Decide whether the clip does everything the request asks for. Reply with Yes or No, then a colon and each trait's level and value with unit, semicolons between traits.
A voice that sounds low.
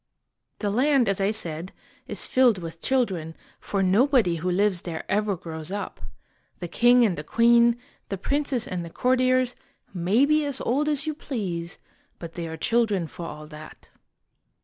No: high, 200 Hz